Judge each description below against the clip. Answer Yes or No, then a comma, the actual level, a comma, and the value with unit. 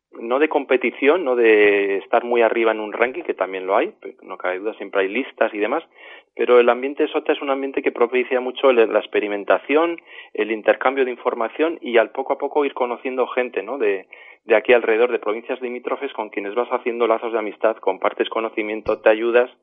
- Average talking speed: No, fast, 205 wpm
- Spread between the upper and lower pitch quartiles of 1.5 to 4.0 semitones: No, average, 4.4 semitones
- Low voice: Yes, low, 125 Hz